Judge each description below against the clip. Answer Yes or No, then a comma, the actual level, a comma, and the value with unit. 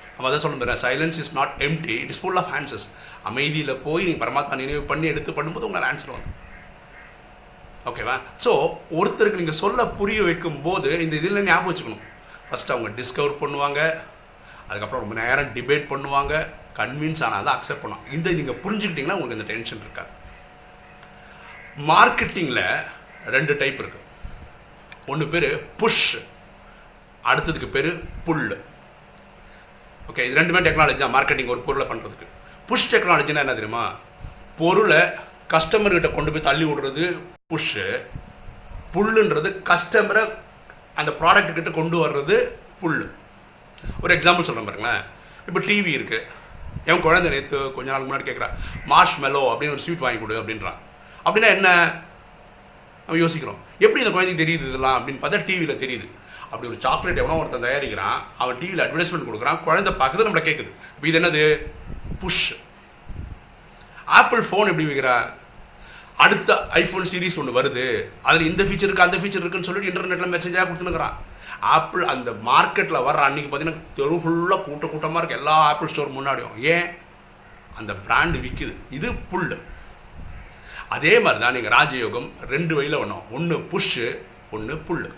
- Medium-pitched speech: Yes, medium, 165 Hz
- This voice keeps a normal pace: No, fast, 140 wpm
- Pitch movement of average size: Yes, average, 4.3 semitones